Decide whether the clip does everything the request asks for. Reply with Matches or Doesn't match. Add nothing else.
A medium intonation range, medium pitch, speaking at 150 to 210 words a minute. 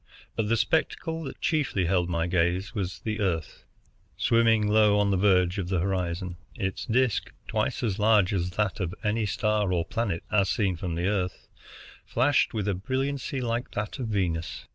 Doesn't match